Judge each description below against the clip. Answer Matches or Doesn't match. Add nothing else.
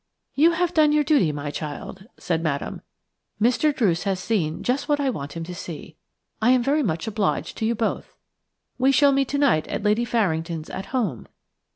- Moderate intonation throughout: Doesn't match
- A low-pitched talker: Doesn't match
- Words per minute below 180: Doesn't match